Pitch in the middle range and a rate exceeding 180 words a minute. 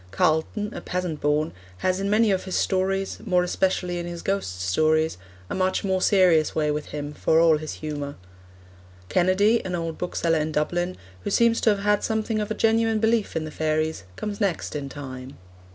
Yes: medium, 175 Hz; average, 190 wpm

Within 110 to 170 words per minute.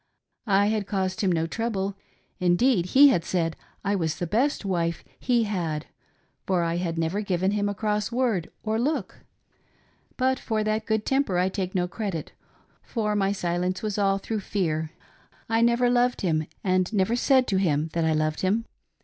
No: average, 180 wpm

